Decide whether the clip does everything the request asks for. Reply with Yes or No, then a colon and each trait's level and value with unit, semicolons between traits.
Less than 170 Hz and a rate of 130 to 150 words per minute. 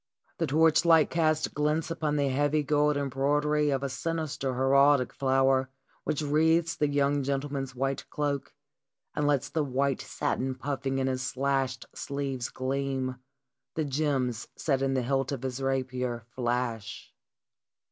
Yes: medium, 140 Hz; average, 140 wpm